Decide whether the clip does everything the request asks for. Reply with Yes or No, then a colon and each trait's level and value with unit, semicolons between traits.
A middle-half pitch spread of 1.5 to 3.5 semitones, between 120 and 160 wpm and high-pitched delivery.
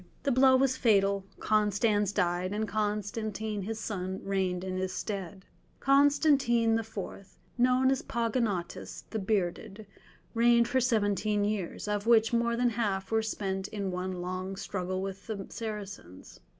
Yes: average, 3.2 semitones; average, 140 wpm; high, 210 Hz